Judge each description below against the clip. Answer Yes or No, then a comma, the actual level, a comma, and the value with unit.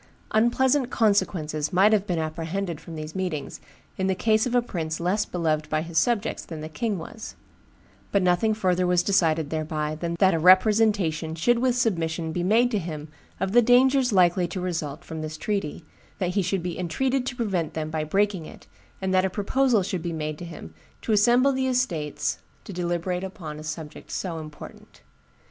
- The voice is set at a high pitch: No, medium, 180 Hz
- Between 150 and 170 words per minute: No, average, 190 wpm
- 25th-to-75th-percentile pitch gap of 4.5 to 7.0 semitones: Yes, average, 5.0 semitones